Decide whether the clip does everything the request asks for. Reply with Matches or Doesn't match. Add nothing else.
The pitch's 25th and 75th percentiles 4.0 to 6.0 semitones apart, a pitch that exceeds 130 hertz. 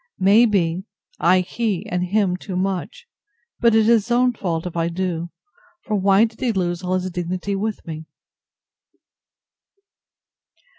Doesn't match